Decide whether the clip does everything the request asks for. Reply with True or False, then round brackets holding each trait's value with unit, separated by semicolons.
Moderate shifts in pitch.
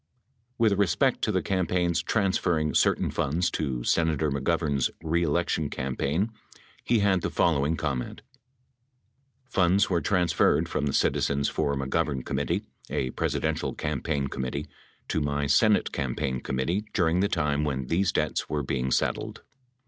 True (4.2 semitones)